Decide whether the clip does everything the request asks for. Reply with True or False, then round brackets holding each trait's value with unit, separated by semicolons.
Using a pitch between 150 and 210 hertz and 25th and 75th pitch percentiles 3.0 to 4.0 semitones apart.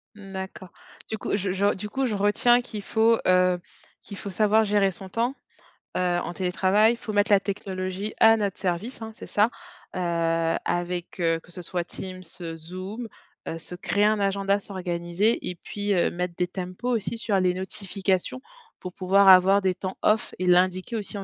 False (190 Hz; 2.4 semitones)